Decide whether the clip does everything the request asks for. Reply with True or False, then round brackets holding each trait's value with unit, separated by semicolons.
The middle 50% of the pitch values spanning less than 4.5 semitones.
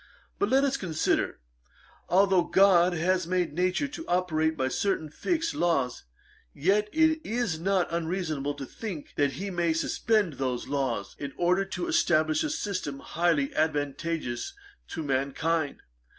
False (4.9 semitones)